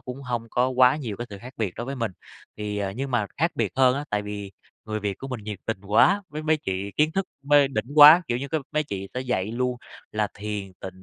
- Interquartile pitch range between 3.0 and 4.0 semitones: No, average, 4.8 semitones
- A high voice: No, low, 120 Hz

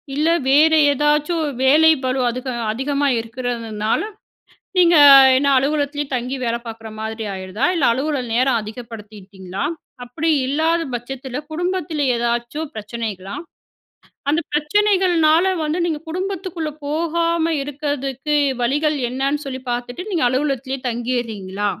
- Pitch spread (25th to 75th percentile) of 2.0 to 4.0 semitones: No, average, 4.7 semitones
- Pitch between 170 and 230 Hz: No, very high, 275 Hz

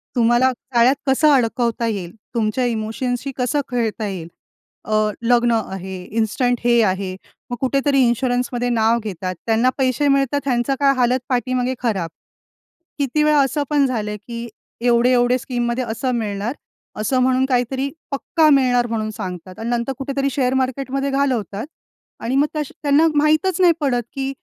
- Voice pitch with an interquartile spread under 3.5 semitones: Yes, average, 3.1 semitones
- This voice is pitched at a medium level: No, high, 245 Hz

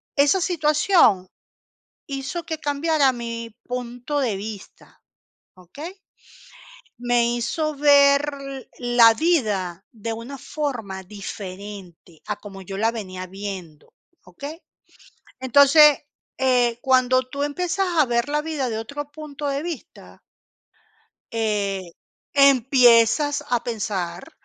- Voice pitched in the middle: No, high, 245 Hz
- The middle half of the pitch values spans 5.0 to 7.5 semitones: Yes, wide, 5.6 semitones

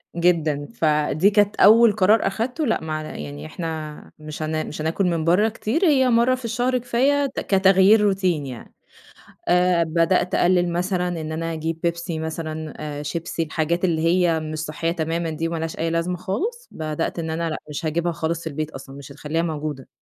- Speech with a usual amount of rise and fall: Yes, average, 3.4 semitones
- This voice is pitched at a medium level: Yes, medium, 165 Hz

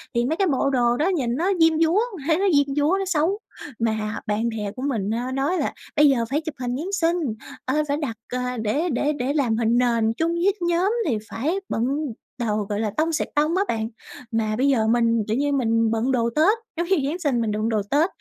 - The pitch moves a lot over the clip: Yes, wide, 5.9 semitones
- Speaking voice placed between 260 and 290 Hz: Yes, very high, 270 Hz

